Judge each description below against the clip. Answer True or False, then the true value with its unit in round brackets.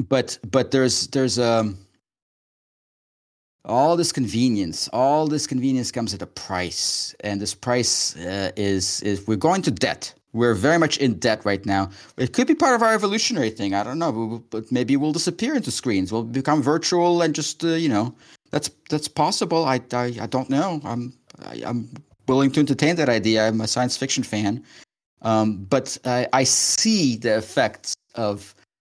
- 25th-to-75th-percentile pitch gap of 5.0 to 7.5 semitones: True (5.6 semitones)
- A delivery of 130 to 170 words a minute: False (185 wpm)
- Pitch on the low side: True (125 Hz)